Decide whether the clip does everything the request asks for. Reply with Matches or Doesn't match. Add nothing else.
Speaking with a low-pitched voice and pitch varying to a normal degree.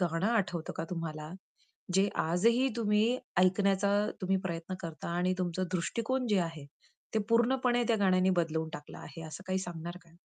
Doesn't match